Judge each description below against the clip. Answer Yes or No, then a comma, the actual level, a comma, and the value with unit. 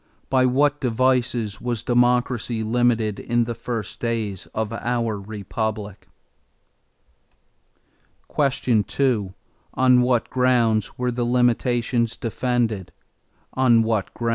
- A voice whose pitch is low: Yes, low, 120 Hz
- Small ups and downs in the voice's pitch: Yes, narrow, 2.1 semitones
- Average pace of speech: No, slow, 90 wpm